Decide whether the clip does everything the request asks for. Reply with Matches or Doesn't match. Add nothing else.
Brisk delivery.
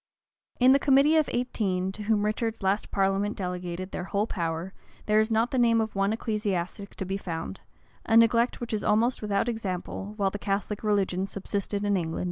Doesn't match